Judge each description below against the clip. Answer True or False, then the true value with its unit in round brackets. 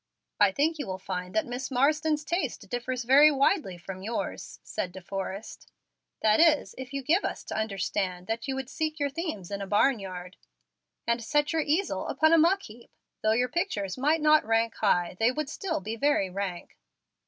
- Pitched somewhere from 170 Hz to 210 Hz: False (245 Hz)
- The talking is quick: False (195 wpm)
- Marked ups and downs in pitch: True (7.4 semitones)